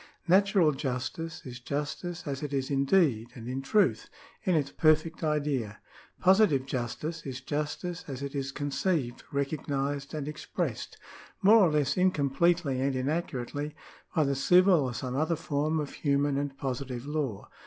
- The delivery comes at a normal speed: Yes, average, 155 wpm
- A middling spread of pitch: Yes, average, 3.1 semitones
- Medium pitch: Yes, medium, 145 Hz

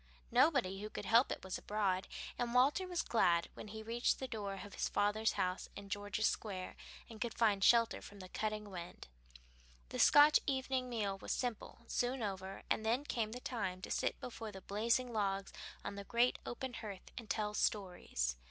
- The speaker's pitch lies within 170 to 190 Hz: No, high, 215 Hz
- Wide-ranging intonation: No, average, 3.5 semitones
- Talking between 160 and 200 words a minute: Yes, average, 190 wpm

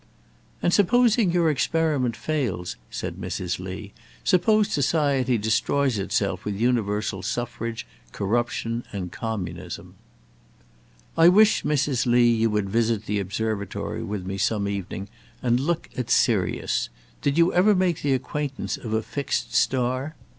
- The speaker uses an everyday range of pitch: No, wide, 6.2 semitones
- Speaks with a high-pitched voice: No, low, 120 Hz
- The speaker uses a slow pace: Yes, slow, 130 wpm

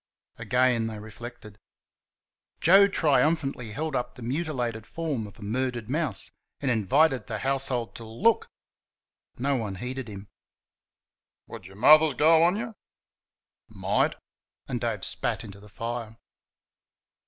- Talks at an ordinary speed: No, slow, 130 wpm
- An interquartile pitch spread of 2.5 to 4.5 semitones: No, average, 5.2 semitones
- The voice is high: No, low, 125 Hz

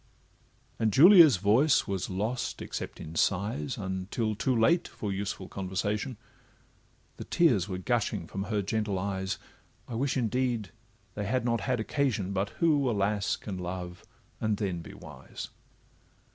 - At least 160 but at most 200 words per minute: No, average, 145 wpm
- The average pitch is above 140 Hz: No, low, 105 Hz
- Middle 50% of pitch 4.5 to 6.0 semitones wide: No, average, 4.1 semitones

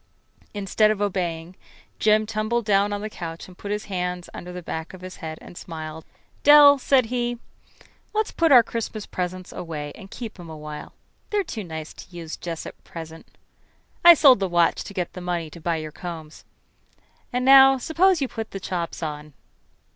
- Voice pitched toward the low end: No, medium, 185 Hz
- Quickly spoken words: No, average, 190 wpm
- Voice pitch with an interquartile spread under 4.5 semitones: No, wide, 5.6 semitones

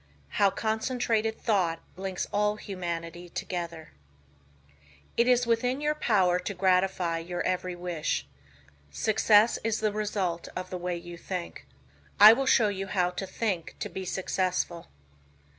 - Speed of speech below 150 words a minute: Yes, average, 140 wpm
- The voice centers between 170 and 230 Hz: Yes, high, 190 Hz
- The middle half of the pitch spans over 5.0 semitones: No, average, 3.5 semitones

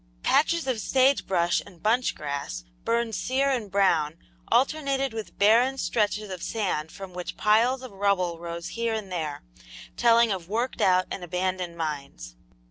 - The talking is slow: No, average, 155 wpm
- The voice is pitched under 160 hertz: No, high, 200 Hz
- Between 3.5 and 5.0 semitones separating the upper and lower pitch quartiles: No, wide, 5.4 semitones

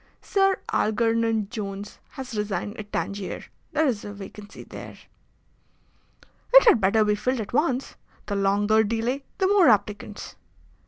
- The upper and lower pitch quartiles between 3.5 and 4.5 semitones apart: Yes, average, 3.8 semitones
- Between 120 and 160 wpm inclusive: Yes, average, 140 wpm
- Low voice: No, high, 220 Hz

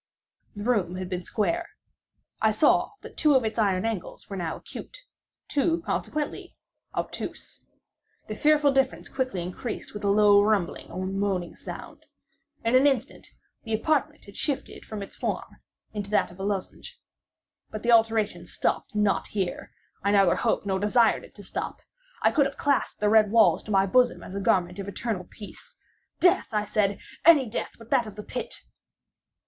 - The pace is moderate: Yes, average, 170 wpm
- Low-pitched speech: No, high, 215 Hz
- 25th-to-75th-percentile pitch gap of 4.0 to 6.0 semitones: Yes, average, 4.4 semitones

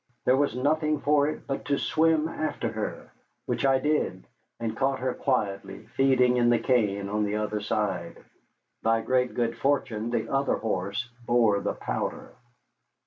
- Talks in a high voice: No, low, 125 Hz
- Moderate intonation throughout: Yes, average, 4.5 semitones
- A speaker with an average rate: Yes, average, 160 wpm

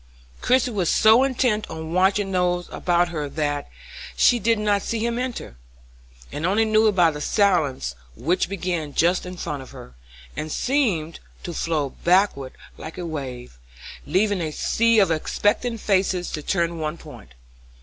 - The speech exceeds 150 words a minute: Yes, average, 160 wpm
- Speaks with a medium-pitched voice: Yes, medium, 180 Hz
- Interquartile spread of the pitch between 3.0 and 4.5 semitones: No, average, 5.2 semitones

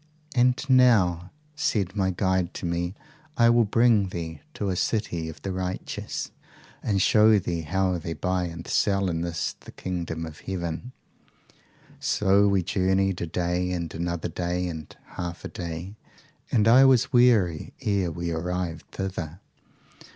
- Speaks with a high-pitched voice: No, very low, 90 Hz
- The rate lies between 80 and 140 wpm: No, average, 150 wpm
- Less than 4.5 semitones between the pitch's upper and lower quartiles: Yes, average, 2.9 semitones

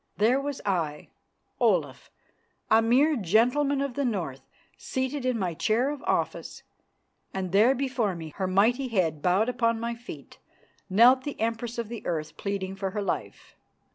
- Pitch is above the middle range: Yes, high, 225 Hz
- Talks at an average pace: Yes, average, 160 wpm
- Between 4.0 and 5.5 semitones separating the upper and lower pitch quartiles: Yes, average, 5.0 semitones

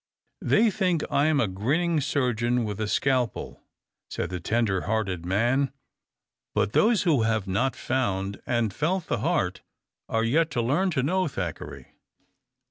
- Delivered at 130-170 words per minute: Yes, average, 150 wpm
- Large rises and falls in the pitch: Yes, wide, 6.5 semitones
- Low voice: Yes, low, 125 Hz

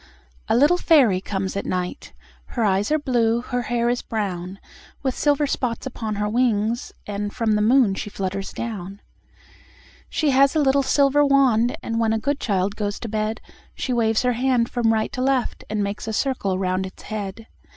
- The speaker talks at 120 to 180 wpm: No, average, 190 wpm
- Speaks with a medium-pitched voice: No, high, 225 Hz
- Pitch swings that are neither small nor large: Yes, average, 4.0 semitones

